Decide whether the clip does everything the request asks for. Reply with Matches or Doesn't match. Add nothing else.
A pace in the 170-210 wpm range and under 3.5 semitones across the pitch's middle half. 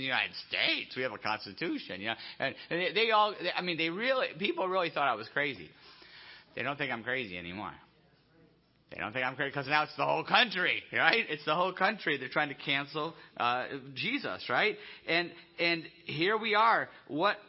Doesn't match